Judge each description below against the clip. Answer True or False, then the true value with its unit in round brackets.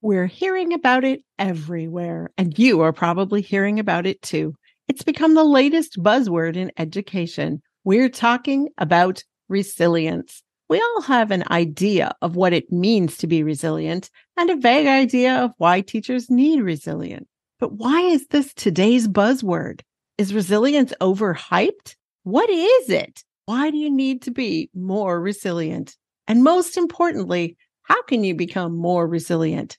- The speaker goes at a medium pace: True (150 wpm)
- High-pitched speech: True (205 Hz)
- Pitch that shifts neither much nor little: False (7.3 semitones)